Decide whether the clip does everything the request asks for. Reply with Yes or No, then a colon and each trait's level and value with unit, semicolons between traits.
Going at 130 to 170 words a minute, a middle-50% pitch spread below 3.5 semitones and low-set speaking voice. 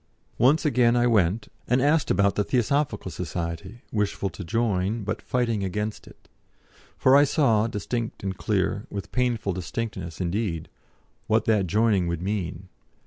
No: average, 145 wpm; average, 4.0 semitones; low, 105 Hz